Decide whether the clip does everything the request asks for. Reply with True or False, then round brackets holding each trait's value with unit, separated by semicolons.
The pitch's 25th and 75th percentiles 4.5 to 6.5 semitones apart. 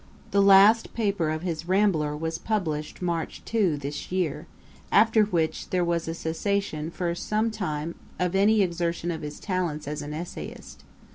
False (4.0 semitones)